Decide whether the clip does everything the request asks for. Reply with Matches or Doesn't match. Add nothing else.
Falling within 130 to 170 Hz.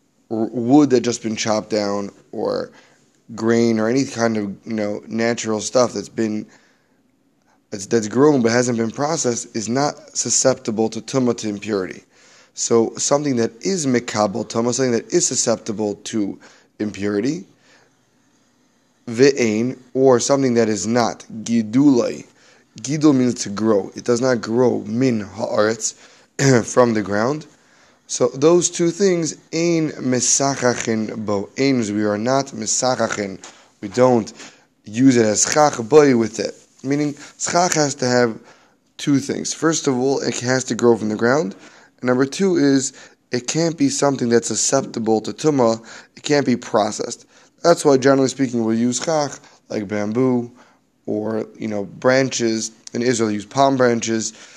Doesn't match